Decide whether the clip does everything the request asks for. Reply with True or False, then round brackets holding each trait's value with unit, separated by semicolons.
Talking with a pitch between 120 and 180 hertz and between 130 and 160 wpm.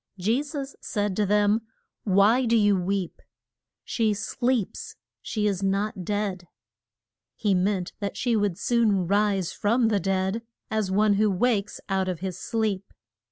False (205 Hz; 150 wpm)